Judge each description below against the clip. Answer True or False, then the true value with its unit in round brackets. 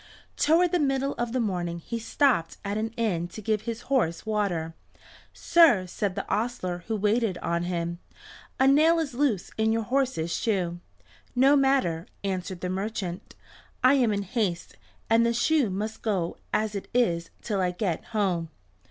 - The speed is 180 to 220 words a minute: False (170 wpm)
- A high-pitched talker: True (215 Hz)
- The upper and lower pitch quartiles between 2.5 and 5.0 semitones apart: False (5.5 semitones)